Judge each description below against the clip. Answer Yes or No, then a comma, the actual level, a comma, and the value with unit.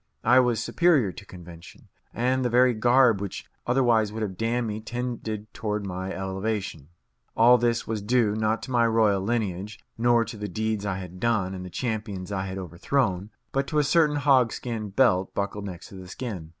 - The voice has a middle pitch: No, low, 110 Hz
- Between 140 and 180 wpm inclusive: No, average, 190 wpm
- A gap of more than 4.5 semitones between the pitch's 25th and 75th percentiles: No, average, 3.9 semitones